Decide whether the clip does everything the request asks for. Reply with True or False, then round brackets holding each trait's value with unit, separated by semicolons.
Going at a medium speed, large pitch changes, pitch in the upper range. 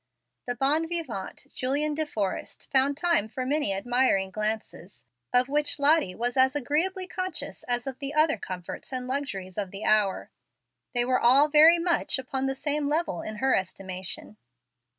True (165 wpm; 5.8 semitones; 265 Hz)